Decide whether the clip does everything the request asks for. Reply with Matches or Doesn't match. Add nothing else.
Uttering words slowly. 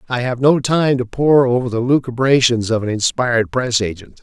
Doesn't match